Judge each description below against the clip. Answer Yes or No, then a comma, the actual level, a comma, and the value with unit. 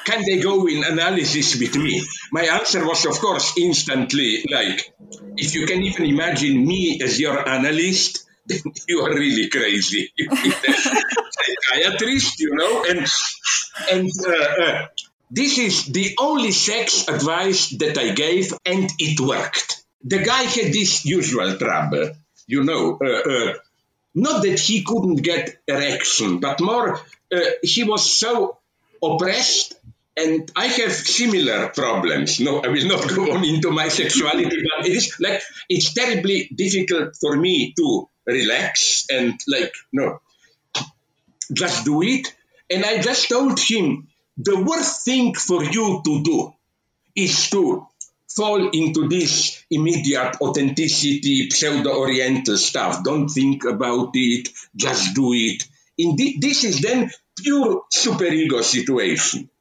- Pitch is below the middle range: No, medium, 185 Hz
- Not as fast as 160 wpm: Yes, average, 140 wpm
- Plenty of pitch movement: Yes, wide, 7.5 semitones